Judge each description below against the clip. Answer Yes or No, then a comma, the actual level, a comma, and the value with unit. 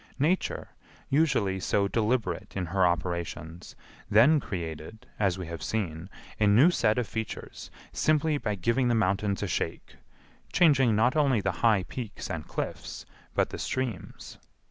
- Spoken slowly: No, average, 145 wpm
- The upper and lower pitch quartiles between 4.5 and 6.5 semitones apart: Yes, wide, 5.5 semitones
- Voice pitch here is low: Yes, low, 105 Hz